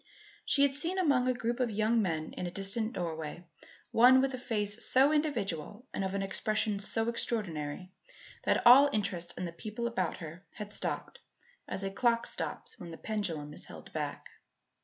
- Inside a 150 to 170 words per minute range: No, average, 180 wpm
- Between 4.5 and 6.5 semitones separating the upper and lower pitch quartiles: Yes, average, 4.9 semitones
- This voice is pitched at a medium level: No, high, 210 Hz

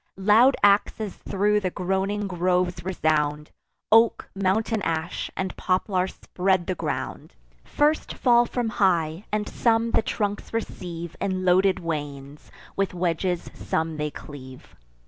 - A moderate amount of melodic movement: Yes, average, 3.7 semitones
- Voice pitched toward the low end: No, medium, 185 Hz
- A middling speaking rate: No, slow, 125 wpm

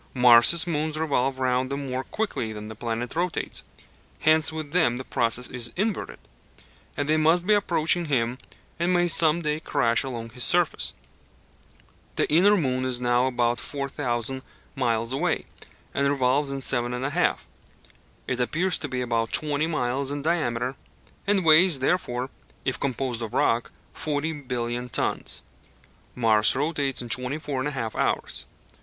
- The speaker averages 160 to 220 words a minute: No, average, 150 wpm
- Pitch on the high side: No, low, 135 Hz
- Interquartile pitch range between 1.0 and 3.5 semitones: No, average, 4.3 semitones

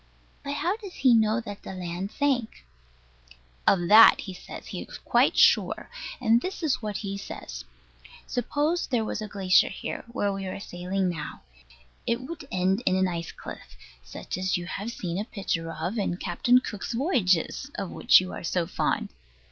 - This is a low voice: No, high, 200 Hz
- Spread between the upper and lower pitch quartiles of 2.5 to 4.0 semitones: No, average, 4.9 semitones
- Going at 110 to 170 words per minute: No, average, 180 wpm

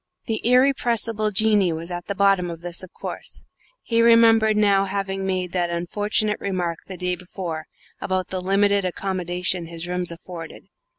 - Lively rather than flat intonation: No, average, 2.9 semitones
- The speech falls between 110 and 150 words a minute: No, average, 160 wpm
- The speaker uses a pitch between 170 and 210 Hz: Yes, high, 190 Hz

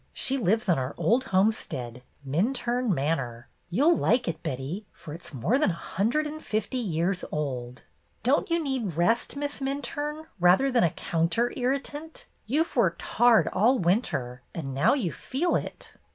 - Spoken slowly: No, average, 165 wpm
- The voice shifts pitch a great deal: Yes, wide, 8.4 semitones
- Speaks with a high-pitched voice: Yes, high, 215 Hz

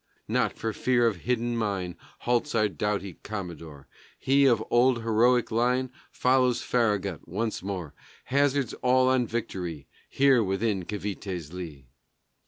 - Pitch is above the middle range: No, low, 110 Hz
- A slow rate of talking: Yes, slow, 130 wpm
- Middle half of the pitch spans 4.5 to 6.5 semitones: Yes, average, 4.8 semitones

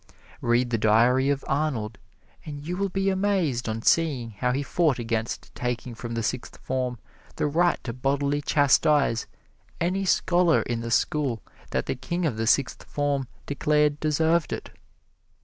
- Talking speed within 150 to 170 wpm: Yes, average, 160 wpm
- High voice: No, medium, 140 Hz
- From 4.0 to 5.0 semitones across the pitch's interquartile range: Yes, average, 4.7 semitones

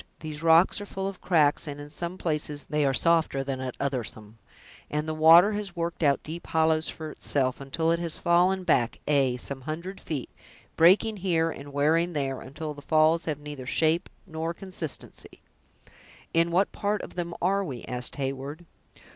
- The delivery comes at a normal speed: Yes, average, 180 wpm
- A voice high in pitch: No, medium, 160 Hz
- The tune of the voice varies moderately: Yes, average, 3.3 semitones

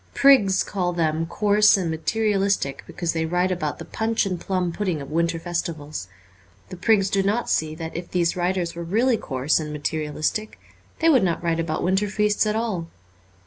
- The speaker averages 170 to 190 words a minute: Yes, average, 185 wpm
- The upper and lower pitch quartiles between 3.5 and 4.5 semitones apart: Yes, average, 4.0 semitones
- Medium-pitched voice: Yes, medium, 175 Hz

